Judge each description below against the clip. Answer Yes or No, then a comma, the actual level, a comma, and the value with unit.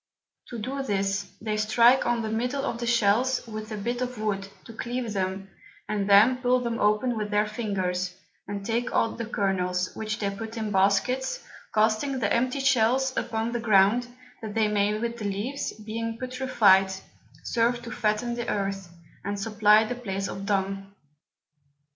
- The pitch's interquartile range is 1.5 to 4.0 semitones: Yes, average, 3.1 semitones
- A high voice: Yes, high, 215 Hz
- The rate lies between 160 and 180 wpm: Yes, average, 170 wpm